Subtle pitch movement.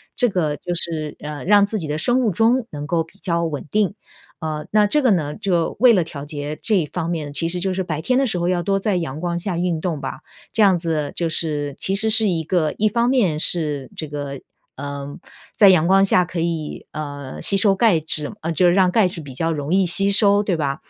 No: average, 4.5 semitones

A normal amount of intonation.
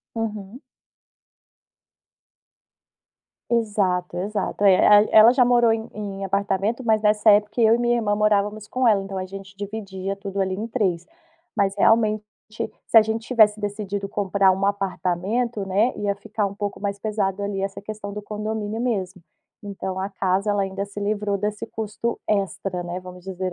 No: narrow, 1.8 semitones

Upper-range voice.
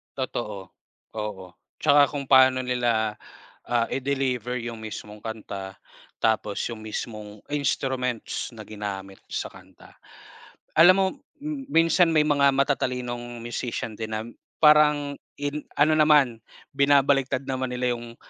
No: low, 125 Hz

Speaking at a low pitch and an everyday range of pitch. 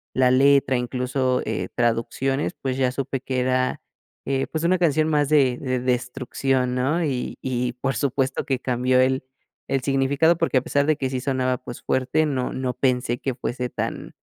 No: low, 130 Hz; narrow, 1.5 semitones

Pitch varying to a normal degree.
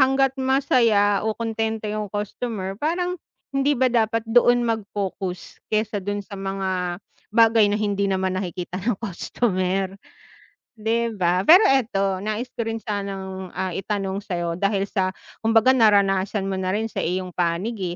Yes: average, 3.2 semitones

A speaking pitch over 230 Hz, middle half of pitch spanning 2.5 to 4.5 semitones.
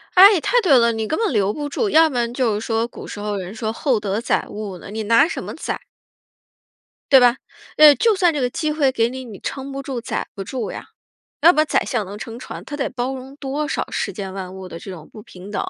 No: high, 245 Hz; wide, 5.5 semitones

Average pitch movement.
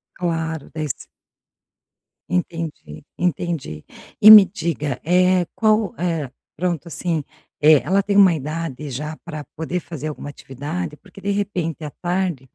Yes: average, 3.3 semitones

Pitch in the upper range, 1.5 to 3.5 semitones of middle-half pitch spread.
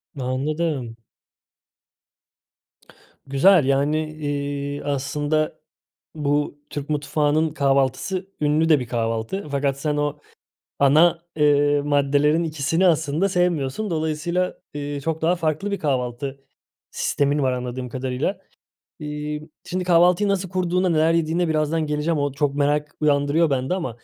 No: medium, 150 Hz; narrow, 2.5 semitones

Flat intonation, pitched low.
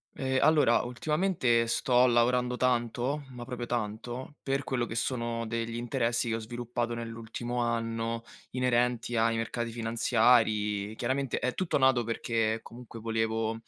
Yes: narrow, 1.6 semitones; low, 120 Hz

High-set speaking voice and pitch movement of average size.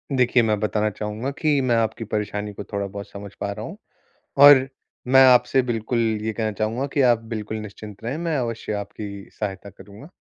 No: low, 110 Hz; average, 3.2 semitones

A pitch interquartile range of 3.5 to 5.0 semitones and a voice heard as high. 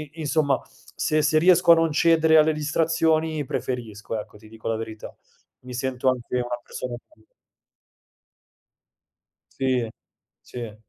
No: average, 4.6 semitones; low, 135 Hz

